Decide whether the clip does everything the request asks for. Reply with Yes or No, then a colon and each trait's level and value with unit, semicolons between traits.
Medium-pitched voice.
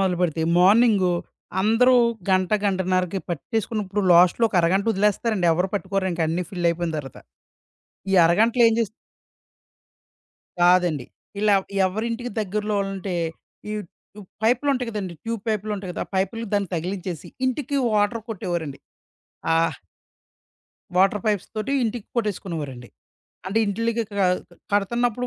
No: high, 195 Hz